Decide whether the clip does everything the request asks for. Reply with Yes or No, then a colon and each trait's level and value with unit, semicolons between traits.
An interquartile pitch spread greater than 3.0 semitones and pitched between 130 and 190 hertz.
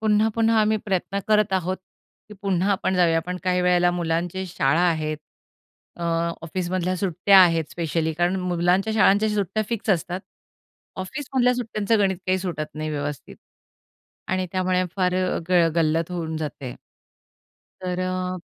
No: narrow, 2.6 semitones; medium, 185 Hz